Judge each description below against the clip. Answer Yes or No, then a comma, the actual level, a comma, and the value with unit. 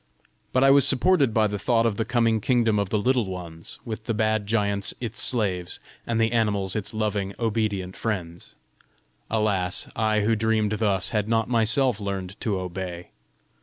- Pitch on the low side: Yes, low, 110 Hz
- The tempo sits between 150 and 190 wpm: Yes, average, 170 wpm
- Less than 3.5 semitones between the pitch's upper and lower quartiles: Yes, narrow, 2.5 semitones